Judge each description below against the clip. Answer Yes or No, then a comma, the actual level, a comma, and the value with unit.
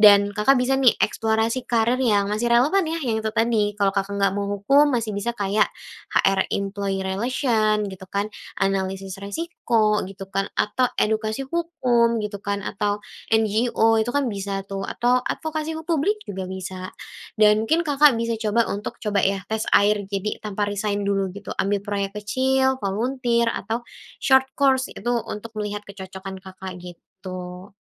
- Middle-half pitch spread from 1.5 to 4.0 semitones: Yes, average, 3.3 semitones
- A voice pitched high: Yes, high, 210 Hz